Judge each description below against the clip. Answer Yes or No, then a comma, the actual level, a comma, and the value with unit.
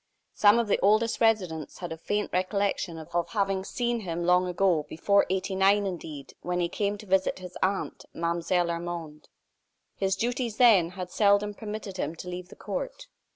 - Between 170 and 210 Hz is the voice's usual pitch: Yes, high, 190 Hz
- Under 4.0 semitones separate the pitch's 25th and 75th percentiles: Yes, average, 3.0 semitones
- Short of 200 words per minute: Yes, average, 170 wpm